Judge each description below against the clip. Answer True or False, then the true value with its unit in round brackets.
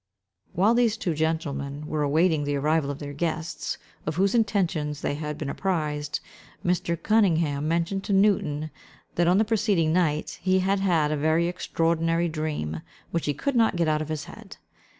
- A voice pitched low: False (165 Hz)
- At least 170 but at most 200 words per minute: True (175 wpm)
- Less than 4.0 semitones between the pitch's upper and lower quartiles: True (3.6 semitones)